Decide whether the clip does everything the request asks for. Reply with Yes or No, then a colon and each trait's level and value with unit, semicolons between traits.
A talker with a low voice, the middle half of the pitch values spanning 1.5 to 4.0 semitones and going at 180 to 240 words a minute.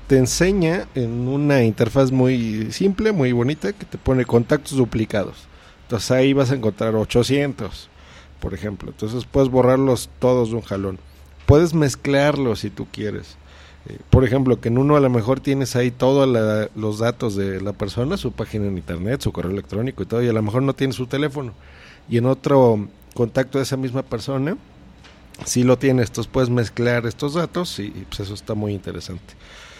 No: low, 120 Hz; average, 4.5 semitones; average, 185 wpm